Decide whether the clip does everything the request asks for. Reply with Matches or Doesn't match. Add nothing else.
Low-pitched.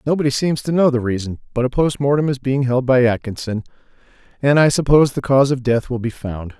Matches